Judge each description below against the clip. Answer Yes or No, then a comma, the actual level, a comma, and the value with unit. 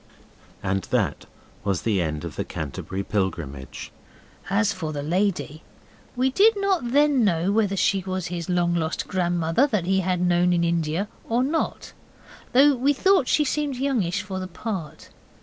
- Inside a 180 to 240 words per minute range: No, average, 165 wpm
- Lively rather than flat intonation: Yes, wide, 7.1 semitones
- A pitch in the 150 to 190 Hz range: Yes, medium, 185 Hz